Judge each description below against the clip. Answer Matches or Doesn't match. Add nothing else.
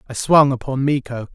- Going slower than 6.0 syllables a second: Matches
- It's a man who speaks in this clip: Matches